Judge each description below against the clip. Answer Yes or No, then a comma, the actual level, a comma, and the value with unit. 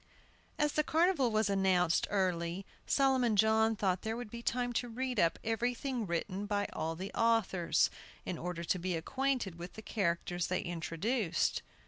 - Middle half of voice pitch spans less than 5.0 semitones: No, average, 5.3 semitones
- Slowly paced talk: No, average, 160 wpm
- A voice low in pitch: No, high, 205 Hz